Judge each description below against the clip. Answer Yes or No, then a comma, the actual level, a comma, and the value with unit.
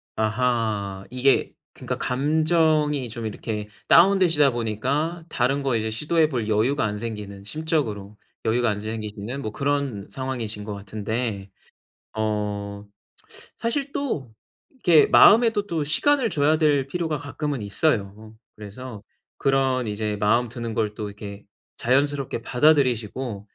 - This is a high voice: No, low, 120 Hz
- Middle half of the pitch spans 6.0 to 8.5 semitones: No, wide, 5.6 semitones